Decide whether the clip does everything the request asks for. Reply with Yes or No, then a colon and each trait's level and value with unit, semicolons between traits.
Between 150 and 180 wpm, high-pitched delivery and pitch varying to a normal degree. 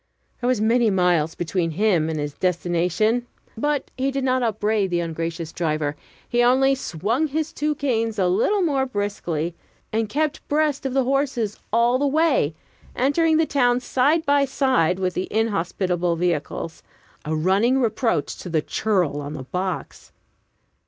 No: average, 160 wpm; high, 220 Hz; wide, 7.4 semitones